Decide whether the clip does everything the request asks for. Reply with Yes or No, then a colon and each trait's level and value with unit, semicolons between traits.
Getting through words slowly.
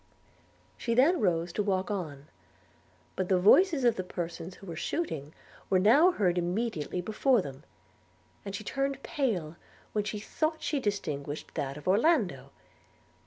No: average, 150 wpm